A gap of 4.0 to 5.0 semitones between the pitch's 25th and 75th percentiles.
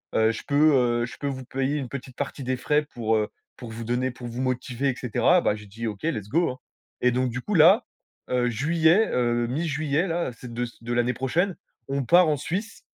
Yes: average, 4.3 semitones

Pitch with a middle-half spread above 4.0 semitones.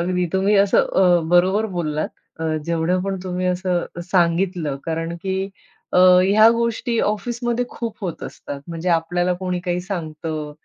No: narrow, 2.4 semitones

